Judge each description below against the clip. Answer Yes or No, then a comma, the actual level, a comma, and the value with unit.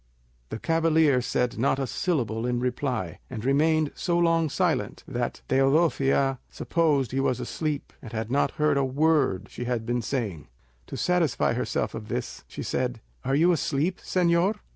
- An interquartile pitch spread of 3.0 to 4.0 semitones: No, average, 4.7 semitones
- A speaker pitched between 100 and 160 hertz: Yes, low, 135 Hz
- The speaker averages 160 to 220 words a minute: Yes, average, 165 wpm